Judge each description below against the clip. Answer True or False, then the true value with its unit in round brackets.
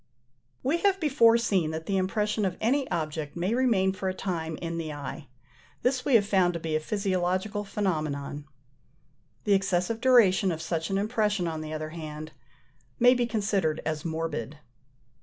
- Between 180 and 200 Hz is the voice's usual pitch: True (185 Hz)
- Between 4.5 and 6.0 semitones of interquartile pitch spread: True (5.1 semitones)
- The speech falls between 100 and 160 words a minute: False (175 wpm)